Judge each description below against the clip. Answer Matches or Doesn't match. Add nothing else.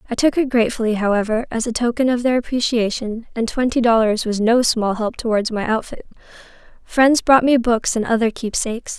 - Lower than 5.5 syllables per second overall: Doesn't match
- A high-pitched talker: Matches